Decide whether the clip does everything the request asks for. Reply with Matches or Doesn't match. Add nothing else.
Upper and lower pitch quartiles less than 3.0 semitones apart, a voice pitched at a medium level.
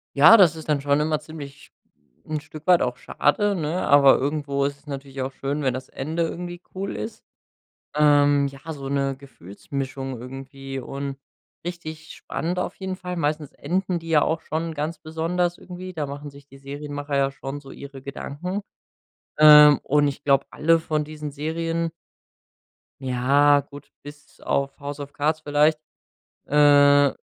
Matches